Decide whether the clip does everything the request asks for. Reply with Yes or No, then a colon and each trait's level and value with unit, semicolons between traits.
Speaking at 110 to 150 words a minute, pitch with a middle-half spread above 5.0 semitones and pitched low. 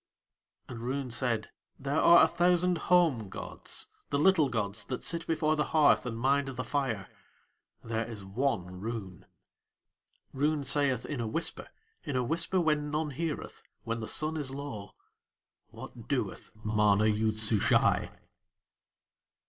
Yes: average, 140 wpm; wide, 5.5 semitones; low, 130 Hz